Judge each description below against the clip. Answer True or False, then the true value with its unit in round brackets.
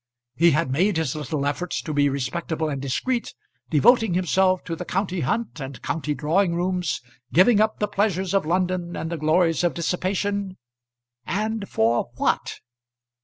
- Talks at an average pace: True (160 wpm)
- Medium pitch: True (175 Hz)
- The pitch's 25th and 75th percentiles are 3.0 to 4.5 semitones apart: True (4.0 semitones)